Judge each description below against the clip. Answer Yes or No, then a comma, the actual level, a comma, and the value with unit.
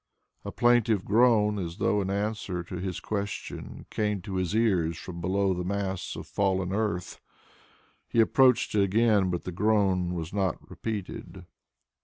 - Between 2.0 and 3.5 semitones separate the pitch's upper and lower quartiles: Yes, average, 2.7 semitones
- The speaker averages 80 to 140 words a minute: No, average, 155 wpm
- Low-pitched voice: Yes, low, 100 Hz